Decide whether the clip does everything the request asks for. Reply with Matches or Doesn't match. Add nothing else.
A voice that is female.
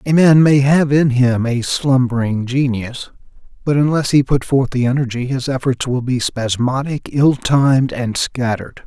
Doesn't match